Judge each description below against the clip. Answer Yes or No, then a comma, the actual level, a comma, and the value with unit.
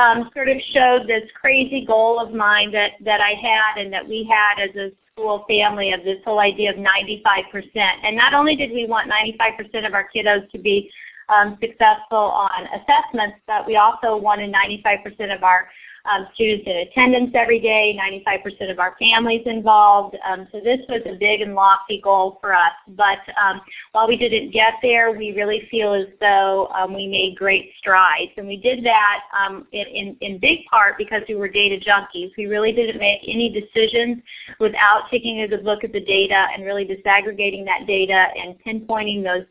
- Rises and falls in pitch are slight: Yes, narrow, 2.2 semitones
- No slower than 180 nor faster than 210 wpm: Yes, average, 200 wpm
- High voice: Yes, high, 210 Hz